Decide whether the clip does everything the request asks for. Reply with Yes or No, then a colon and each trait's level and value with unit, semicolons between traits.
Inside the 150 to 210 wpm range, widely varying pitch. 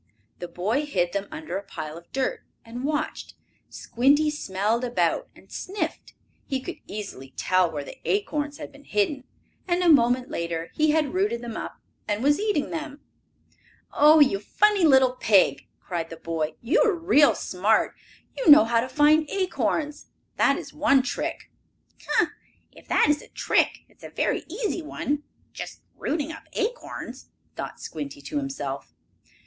Yes: average, 165 wpm; wide, 6.6 semitones